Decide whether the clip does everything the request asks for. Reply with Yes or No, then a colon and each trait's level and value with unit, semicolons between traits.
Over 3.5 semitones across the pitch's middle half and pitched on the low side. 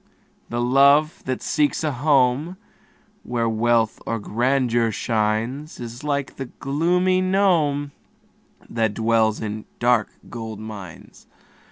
Yes: average, 4.4 semitones; low, 125 Hz